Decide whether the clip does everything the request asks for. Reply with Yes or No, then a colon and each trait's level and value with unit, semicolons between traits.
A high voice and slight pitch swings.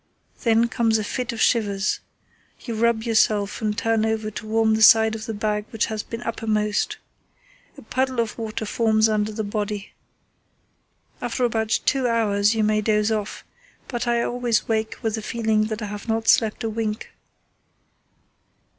Yes: high, 220 Hz; narrow, 1.3 semitones